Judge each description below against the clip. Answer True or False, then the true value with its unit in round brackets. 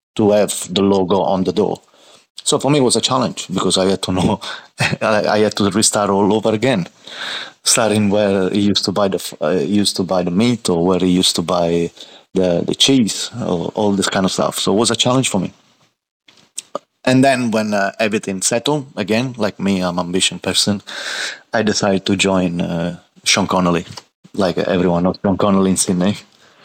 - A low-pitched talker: True (100 Hz)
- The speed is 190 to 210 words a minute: True (200 wpm)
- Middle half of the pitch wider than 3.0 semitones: False (2.4 semitones)